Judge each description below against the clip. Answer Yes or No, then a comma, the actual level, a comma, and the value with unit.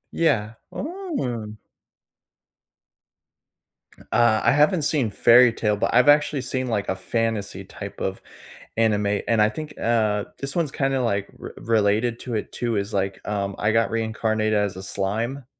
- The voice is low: Yes, low, 115 Hz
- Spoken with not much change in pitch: No, average, 3.6 semitones